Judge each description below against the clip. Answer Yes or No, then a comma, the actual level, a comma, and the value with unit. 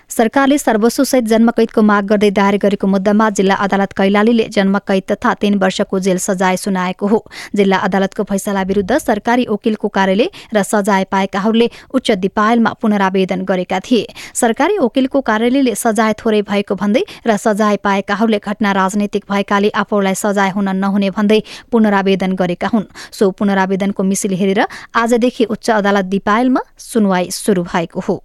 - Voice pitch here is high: Yes, high, 205 Hz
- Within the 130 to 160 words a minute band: Yes, average, 145 wpm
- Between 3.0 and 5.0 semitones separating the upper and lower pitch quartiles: No, narrow, 2.4 semitones